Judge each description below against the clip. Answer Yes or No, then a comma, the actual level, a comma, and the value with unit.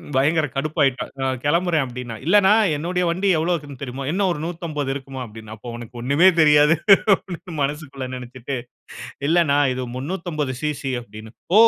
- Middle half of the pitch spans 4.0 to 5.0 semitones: Yes, average, 4.5 semitones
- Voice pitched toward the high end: No, medium, 145 Hz